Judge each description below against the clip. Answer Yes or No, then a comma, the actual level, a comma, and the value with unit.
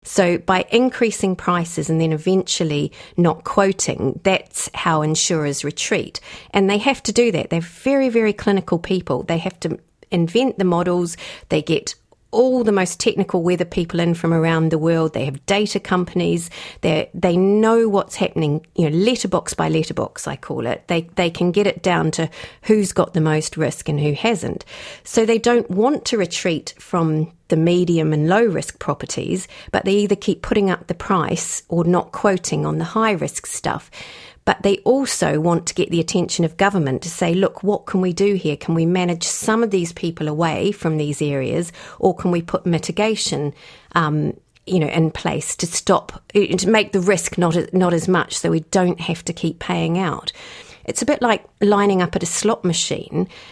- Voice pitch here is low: No, medium, 180 Hz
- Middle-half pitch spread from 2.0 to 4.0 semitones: Yes, average, 3.5 semitones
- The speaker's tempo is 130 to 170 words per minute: No, average, 190 wpm